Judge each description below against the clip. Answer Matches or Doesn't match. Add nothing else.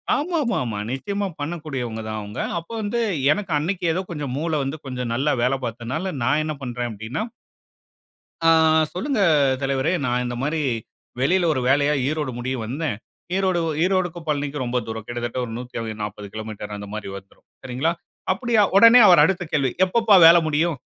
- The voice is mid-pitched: Matches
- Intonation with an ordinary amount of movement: Doesn't match